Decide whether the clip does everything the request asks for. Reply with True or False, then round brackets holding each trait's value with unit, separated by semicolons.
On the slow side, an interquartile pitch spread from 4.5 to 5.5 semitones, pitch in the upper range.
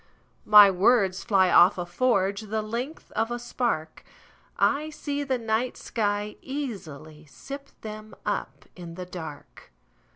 True (120 wpm; 5.0 semitones; 215 Hz)